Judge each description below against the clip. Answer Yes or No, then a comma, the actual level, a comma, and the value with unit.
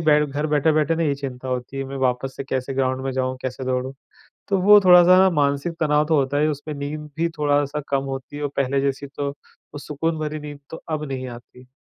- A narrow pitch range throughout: Yes, narrow, 2.3 semitones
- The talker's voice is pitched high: No, medium, 145 Hz